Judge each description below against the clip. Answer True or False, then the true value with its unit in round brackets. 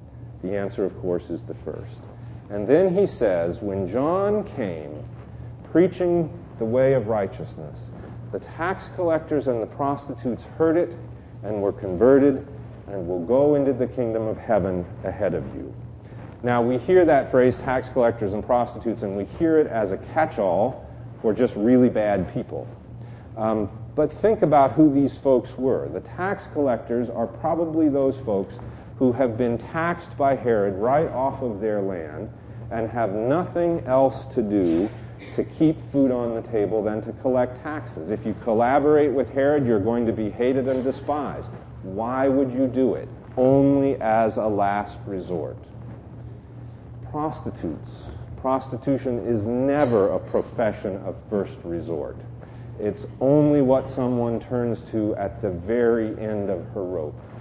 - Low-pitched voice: True (120 Hz)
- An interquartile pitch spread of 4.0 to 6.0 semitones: False (3.6 semitones)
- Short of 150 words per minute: False (155 wpm)